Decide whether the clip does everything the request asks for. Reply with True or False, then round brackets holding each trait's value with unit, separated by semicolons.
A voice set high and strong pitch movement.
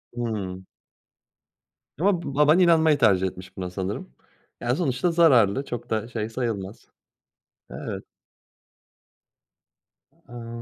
False (120 Hz; 6.9 semitones)